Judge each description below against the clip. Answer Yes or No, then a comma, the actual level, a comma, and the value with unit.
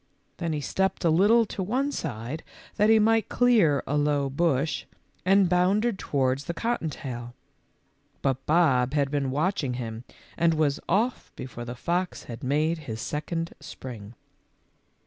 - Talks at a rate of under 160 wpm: Yes, average, 150 wpm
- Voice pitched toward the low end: No, medium, 155 Hz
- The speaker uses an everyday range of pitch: No, wide, 6.0 semitones